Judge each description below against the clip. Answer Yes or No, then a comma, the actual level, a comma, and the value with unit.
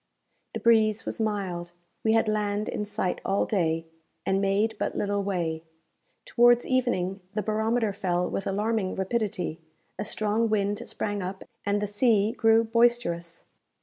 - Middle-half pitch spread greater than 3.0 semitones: No, narrow, 2.5 semitones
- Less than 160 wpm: Yes, average, 150 wpm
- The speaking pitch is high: Yes, high, 205 Hz